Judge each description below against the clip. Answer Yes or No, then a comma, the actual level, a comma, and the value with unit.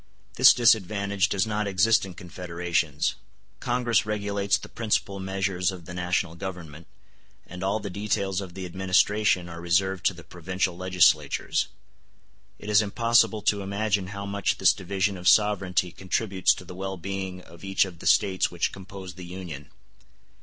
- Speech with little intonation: Yes, narrow, 2.1 semitones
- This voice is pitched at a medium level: No, very low, 95 Hz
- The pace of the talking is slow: No, average, 160 wpm